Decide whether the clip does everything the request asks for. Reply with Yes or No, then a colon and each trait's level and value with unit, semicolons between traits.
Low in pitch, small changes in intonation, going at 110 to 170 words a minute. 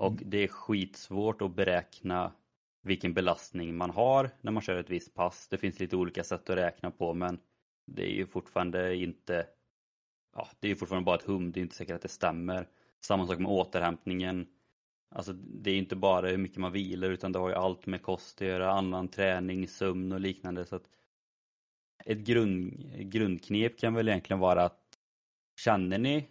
No: very low, 95 Hz; narrow, 1.4 semitones; average, 190 wpm